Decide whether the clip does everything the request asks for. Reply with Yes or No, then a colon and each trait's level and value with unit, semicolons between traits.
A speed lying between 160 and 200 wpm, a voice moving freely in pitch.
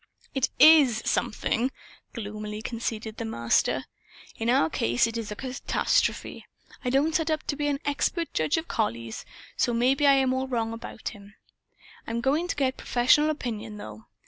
No: average, 170 wpm; average, 4.4 semitones